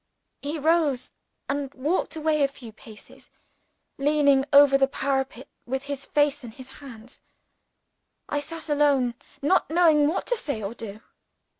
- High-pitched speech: Yes, very high, 280 Hz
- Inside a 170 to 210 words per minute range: No, average, 145 wpm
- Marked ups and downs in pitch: No, narrow, 2.4 semitones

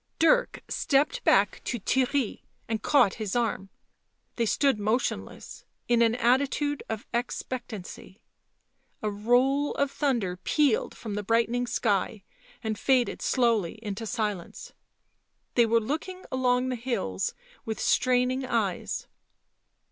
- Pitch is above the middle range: Yes, high, 240 Hz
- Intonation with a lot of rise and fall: No, average, 3.3 semitones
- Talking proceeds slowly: Yes, slow, 120 wpm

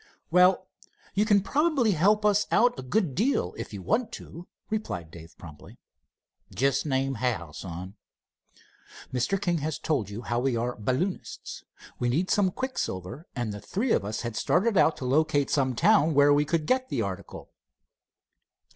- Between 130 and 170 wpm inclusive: Yes, average, 165 wpm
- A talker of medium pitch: Yes, medium, 145 Hz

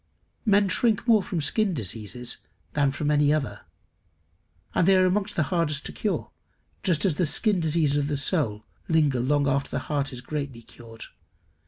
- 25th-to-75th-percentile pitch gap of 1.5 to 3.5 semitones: No, average, 5.2 semitones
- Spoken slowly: No, average, 185 wpm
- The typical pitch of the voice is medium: Yes, medium, 150 Hz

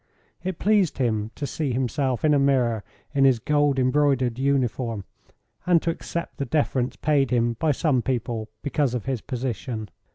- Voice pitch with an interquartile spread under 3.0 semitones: No, average, 3.5 semitones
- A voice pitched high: No, low, 130 Hz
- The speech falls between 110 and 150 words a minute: No, average, 165 wpm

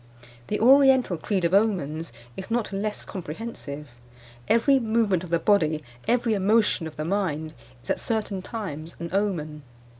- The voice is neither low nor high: No, high, 195 Hz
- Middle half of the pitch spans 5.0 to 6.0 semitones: Yes, wide, 5.6 semitones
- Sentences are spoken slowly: No, average, 150 wpm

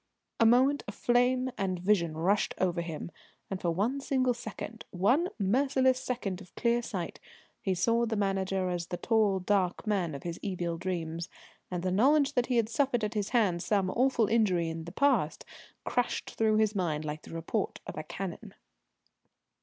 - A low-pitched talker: No, high, 200 Hz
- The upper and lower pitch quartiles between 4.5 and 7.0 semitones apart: Yes, average, 5.3 semitones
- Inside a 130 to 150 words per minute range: No, average, 180 wpm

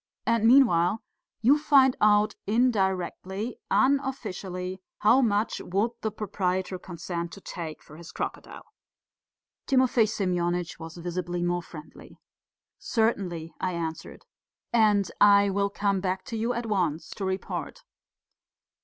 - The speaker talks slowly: Yes, slow, 120 wpm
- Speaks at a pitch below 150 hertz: No, high, 195 Hz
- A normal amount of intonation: Yes, average, 4.1 semitones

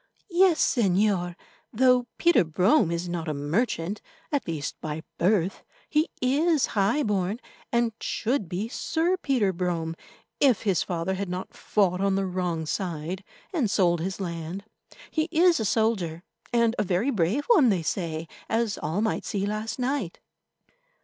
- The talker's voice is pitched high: Yes, high, 195 Hz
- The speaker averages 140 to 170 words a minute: Yes, average, 155 wpm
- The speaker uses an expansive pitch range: Yes, wide, 5.8 semitones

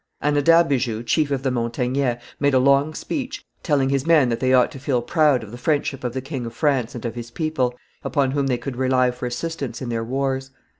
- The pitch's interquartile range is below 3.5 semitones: Yes, narrow, 2.6 semitones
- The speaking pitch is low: Yes, low, 130 Hz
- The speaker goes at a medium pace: No, fast, 220 wpm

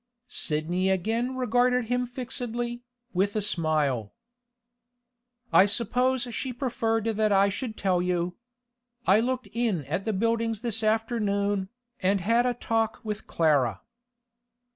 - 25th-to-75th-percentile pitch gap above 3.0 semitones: Yes, average, 4.2 semitones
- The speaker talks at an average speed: No, slow, 125 wpm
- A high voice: Yes, high, 220 Hz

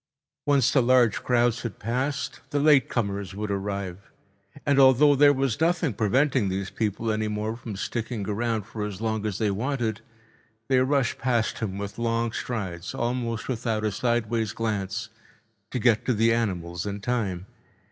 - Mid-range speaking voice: No, low, 115 Hz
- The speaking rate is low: No, average, 160 wpm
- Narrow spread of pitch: No, average, 3.4 semitones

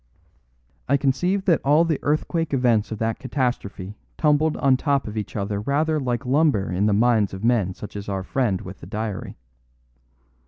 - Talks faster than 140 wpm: Yes, average, 180 wpm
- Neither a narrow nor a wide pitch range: No, wide, 5.8 semitones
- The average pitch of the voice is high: No, low, 120 Hz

